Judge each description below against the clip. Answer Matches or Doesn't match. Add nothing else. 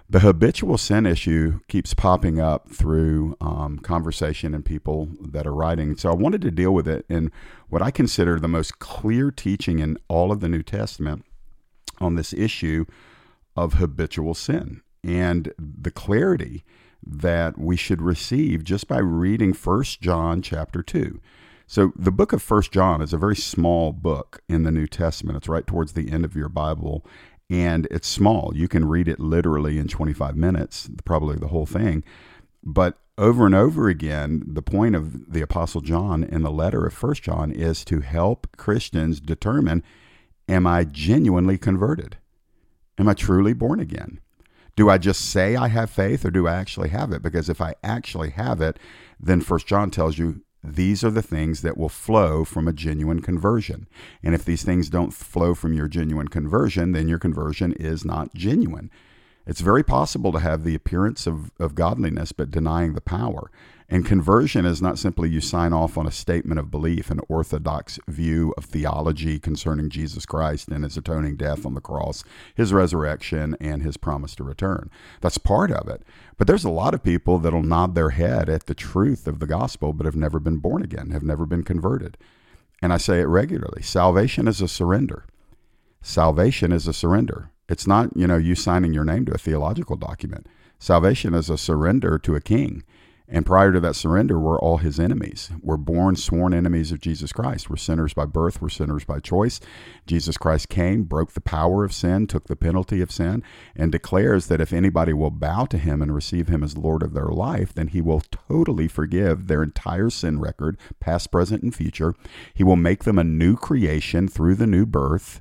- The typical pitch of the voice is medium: Doesn't match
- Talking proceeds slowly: Doesn't match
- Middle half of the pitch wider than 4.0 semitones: Doesn't match